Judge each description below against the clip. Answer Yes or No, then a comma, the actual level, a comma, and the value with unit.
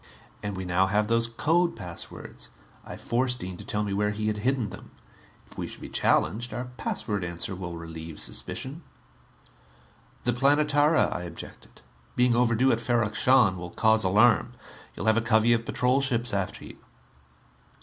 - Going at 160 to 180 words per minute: Yes, average, 170 wpm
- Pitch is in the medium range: No, low, 110 Hz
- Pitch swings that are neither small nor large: Yes, average, 4.3 semitones